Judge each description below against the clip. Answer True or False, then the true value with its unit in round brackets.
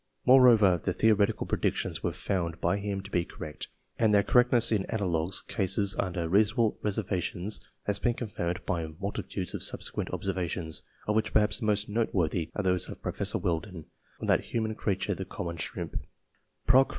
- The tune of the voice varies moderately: True (3.6 semitones)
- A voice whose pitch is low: True (100 Hz)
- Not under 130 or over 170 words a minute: True (165 wpm)